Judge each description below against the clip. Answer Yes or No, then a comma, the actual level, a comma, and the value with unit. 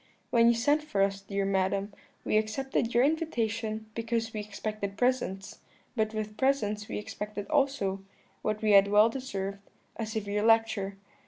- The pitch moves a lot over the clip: No, narrow, 2.6 semitones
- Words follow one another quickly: No, average, 165 wpm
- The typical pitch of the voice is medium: No, high, 215 Hz